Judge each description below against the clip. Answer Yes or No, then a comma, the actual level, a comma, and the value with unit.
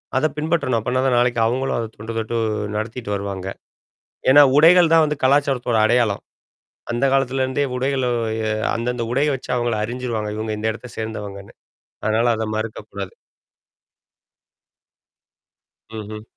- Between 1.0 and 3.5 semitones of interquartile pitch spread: Yes, average, 3.2 semitones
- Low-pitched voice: Yes, low, 120 Hz